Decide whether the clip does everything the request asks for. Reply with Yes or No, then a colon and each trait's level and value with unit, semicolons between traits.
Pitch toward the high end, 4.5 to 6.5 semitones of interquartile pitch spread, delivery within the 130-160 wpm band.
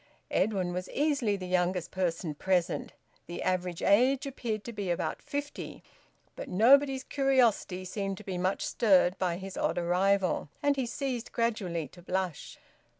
Yes: high, 195 Hz; average, 5.0 semitones; average, 150 wpm